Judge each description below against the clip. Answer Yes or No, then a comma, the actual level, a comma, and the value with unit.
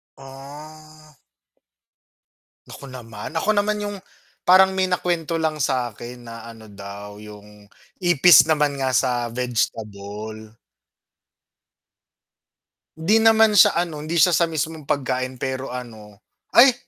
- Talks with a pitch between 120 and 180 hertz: Yes, low, 135 Hz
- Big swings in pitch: Yes, wide, 6.3 semitones